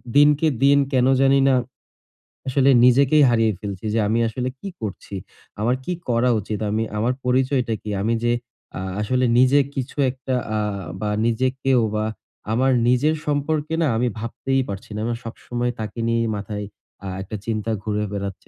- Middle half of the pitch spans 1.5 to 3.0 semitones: No, average, 3.5 semitones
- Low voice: Yes, low, 120 Hz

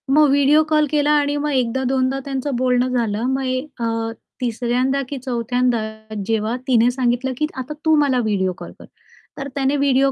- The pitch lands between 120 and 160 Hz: No, very high, 260 Hz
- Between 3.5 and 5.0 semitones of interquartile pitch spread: No, narrow, 2.5 semitones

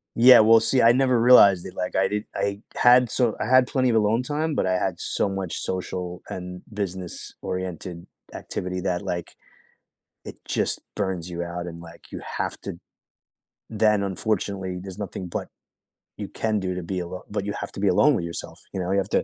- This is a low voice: Yes, very low, 95 Hz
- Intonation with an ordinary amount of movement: Yes, average, 3.5 semitones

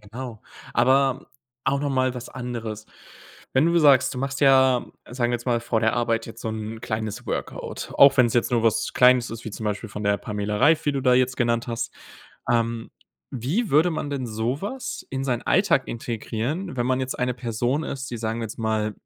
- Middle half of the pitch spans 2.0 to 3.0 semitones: Yes, average, 2.7 semitones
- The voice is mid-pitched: No, low, 120 Hz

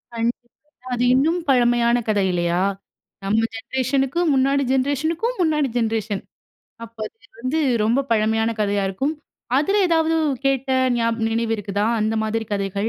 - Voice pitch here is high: Yes, high, 240 Hz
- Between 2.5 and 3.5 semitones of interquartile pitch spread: No, average, 4.0 semitones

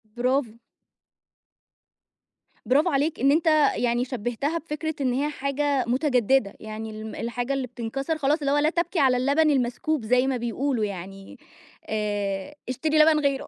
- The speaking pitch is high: Yes, very high, 265 Hz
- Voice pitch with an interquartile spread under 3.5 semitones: No, average, 3.8 semitones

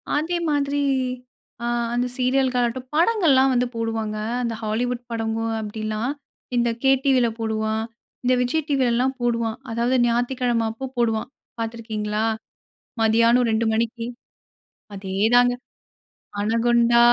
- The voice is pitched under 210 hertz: No, high, 235 Hz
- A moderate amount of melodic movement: No, narrow, 2.2 semitones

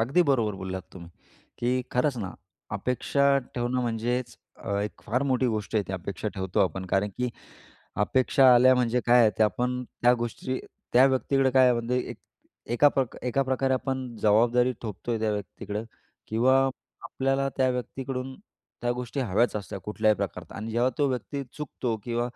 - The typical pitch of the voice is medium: No, low, 120 Hz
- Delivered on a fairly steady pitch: No, average, 3.2 semitones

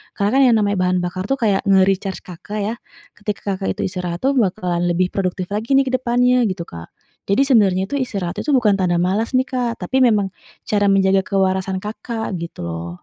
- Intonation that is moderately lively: Yes, average, 3.8 semitones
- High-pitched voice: Yes, high, 195 Hz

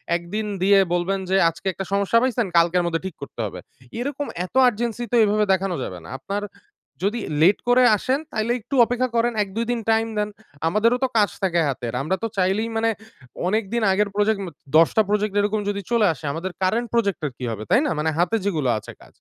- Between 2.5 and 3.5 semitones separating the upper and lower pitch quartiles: No, average, 4.5 semitones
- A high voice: Yes, high, 205 Hz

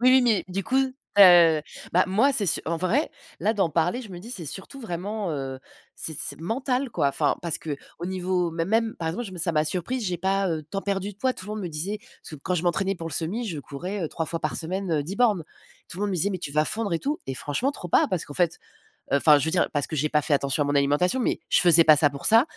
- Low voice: No, medium, 180 Hz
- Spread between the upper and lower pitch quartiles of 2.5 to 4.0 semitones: No, average, 4.6 semitones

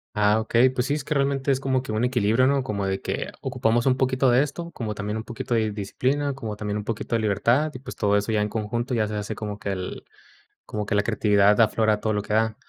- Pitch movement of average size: Yes, average, 3.7 semitones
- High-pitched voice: No, low, 110 Hz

